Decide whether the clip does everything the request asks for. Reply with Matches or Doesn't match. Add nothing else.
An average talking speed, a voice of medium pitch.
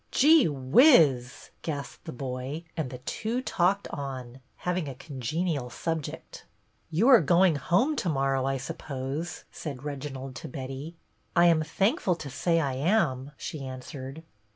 Matches